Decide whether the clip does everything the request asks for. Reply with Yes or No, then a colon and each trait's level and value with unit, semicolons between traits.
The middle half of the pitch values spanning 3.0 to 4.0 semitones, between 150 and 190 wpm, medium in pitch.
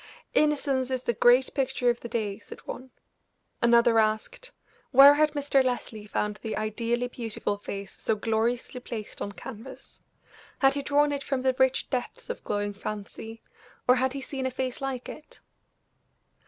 No: average, 3.4 semitones; average, 165 wpm; high, 245 Hz